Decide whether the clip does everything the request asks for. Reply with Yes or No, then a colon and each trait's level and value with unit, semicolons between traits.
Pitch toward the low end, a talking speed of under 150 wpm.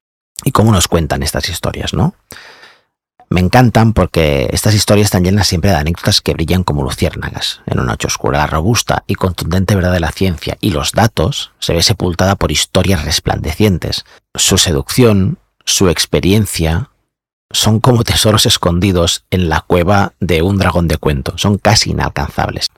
No: very low, 90 Hz; average, 160 wpm